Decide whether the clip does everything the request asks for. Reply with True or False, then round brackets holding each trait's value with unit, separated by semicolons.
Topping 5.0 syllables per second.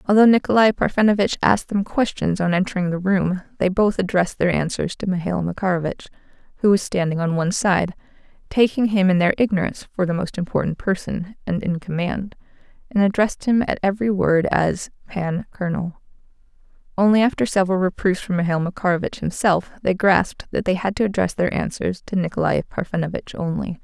True (5.9 syllables/s)